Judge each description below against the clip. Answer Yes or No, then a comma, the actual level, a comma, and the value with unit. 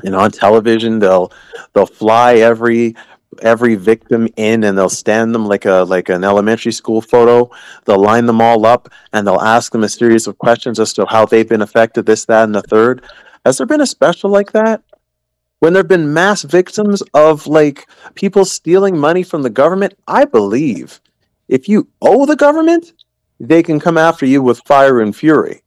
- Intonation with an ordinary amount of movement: No, wide, 7.0 semitones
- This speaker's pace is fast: No, average, 190 wpm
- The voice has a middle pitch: No, low, 120 Hz